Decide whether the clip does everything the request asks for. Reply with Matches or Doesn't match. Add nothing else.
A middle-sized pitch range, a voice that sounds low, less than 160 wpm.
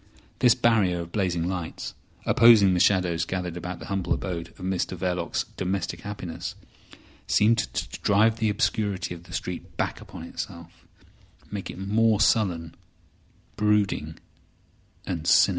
Matches